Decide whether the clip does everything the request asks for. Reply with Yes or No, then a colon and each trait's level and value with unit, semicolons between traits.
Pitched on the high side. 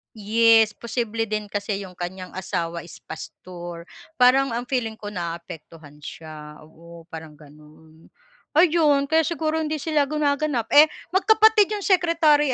Yes: high, 220 Hz